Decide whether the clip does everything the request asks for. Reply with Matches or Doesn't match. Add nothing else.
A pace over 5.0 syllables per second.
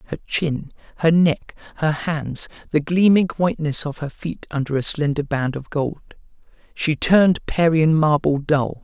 Doesn't match